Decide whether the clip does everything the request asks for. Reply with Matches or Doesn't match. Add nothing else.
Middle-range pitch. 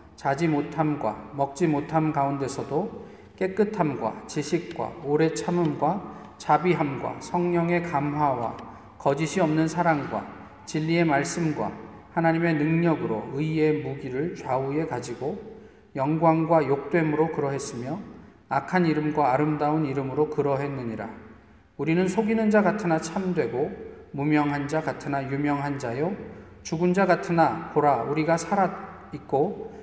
Matches